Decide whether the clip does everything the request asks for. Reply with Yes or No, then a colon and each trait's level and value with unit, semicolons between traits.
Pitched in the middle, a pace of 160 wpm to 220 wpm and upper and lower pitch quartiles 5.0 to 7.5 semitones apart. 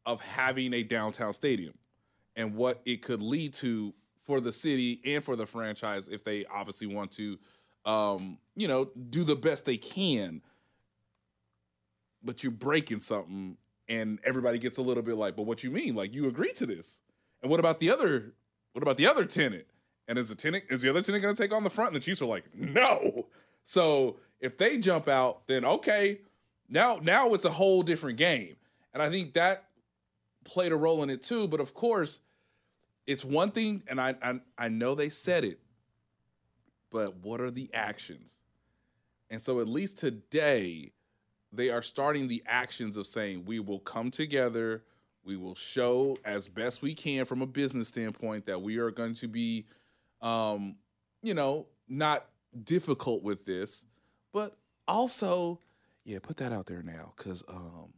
No: low, 125 Hz; average, 180 wpm; average, 5.3 semitones